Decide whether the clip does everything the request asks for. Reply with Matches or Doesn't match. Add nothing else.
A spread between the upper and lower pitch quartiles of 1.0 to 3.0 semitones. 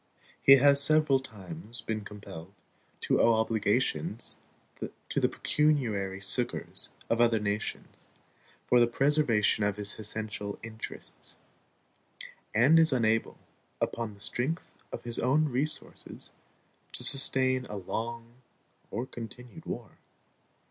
Doesn't match